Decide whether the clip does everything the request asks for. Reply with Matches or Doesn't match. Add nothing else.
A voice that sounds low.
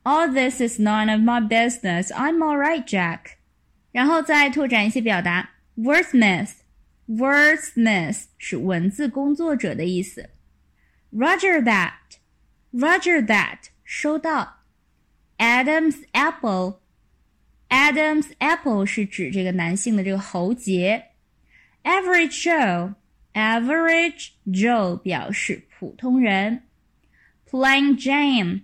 Doesn't match